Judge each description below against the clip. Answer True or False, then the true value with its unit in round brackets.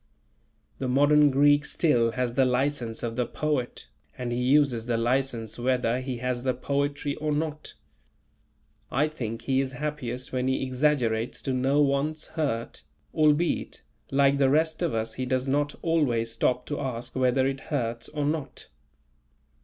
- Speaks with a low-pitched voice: True (130 Hz)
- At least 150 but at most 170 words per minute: True (160 wpm)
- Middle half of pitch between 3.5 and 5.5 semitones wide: False (3.0 semitones)